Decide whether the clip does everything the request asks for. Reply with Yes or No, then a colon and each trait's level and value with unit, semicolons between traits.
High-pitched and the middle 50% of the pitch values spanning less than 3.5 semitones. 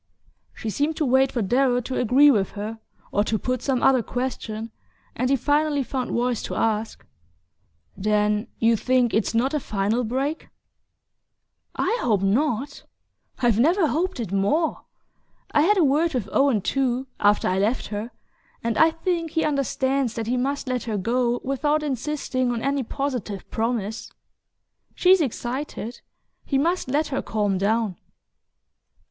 No: very high, 250 Hz; average, 4.2 semitones